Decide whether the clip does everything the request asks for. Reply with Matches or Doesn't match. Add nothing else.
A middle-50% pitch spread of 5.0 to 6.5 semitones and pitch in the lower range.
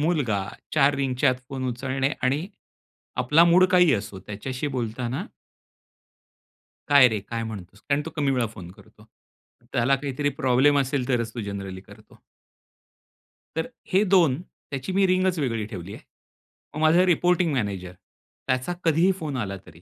Matches